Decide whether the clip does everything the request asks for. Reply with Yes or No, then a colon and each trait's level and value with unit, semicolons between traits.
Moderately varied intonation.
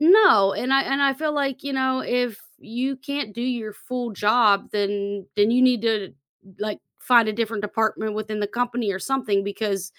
Yes: average, 3.8 semitones